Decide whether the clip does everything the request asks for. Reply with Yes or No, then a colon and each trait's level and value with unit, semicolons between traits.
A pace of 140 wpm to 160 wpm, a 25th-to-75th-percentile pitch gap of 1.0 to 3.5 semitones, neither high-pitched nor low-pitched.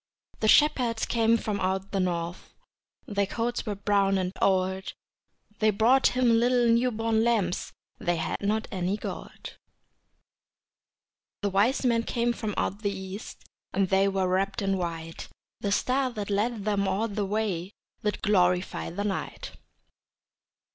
No: average, 150 wpm; average, 3.1 semitones; high, 205 Hz